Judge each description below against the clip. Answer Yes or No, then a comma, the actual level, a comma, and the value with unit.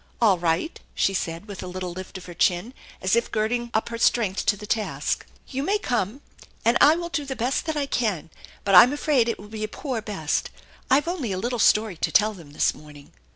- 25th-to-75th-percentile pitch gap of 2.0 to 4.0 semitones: No, average, 5.0 semitones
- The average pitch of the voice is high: Yes, high, 215 Hz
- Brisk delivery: Yes, fast, 220 wpm